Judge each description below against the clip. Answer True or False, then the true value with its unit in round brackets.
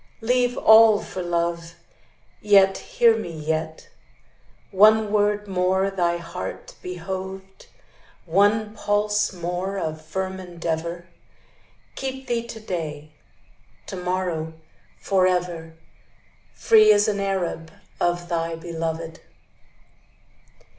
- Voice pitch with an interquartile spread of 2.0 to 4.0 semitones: True (3.5 semitones)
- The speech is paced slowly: True (100 wpm)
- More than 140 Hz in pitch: True (185 Hz)